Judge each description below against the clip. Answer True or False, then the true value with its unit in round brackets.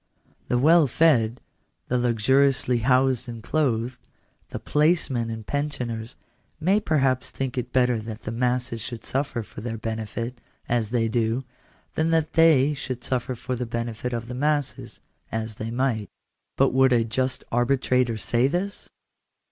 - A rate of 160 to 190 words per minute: False (150 wpm)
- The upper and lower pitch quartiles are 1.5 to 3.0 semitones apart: True (2.7 semitones)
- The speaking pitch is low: True (125 Hz)